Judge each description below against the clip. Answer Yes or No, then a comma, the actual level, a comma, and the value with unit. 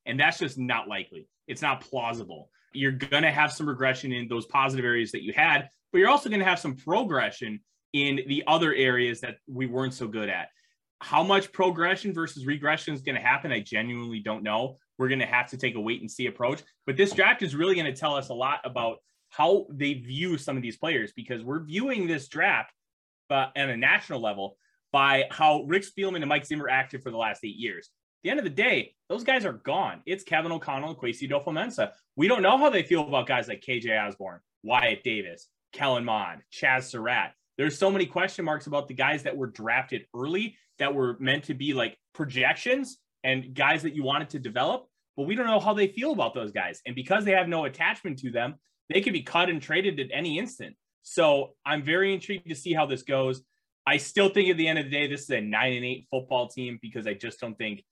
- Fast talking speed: Yes, fast, 225 wpm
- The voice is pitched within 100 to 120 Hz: No, medium, 140 Hz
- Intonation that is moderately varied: Yes, average, 5.0 semitones